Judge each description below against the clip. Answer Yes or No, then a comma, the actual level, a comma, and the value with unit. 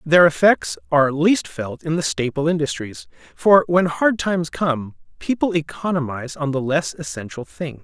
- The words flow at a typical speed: Yes, average, 160 wpm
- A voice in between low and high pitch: Yes, medium, 150 Hz